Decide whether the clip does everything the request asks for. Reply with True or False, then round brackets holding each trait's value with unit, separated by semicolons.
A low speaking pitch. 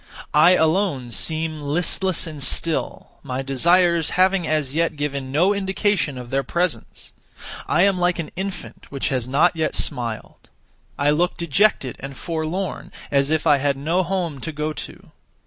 False (160 Hz)